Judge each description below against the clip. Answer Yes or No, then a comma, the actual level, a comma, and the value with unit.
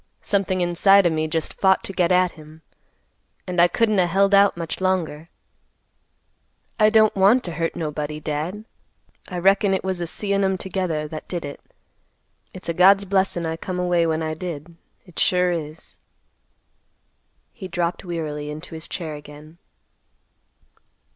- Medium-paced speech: Yes, average, 160 wpm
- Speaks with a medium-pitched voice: Yes, medium, 175 Hz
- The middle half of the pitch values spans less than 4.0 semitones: Yes, average, 3.1 semitones